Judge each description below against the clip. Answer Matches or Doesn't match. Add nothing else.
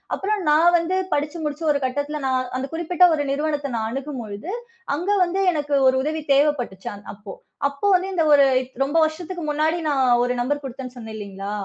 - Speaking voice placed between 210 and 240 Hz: Doesn't match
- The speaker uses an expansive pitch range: Doesn't match